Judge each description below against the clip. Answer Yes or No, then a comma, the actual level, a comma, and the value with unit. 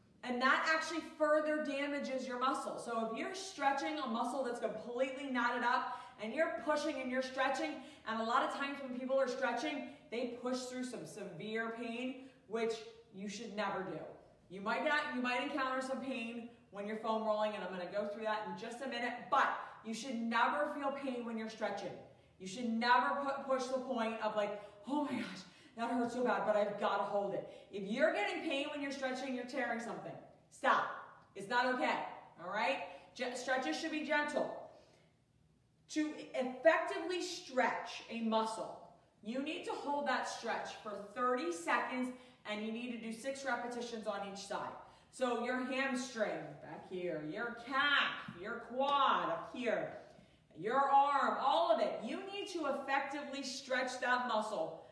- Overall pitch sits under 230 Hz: No, very high, 250 Hz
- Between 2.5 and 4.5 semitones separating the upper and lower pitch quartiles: Yes, average, 3.9 semitones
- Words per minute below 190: Yes, average, 180 wpm